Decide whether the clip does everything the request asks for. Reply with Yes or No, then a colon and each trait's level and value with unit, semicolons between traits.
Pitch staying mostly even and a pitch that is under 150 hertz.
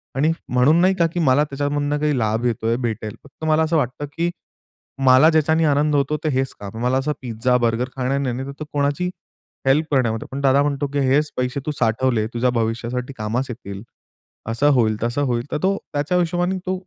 No: average, 3.7 semitones; low, 135 Hz